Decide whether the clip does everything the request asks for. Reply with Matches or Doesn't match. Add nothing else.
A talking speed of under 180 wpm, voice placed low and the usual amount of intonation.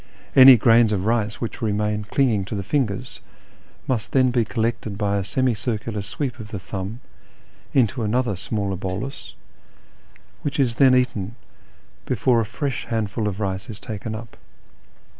Matches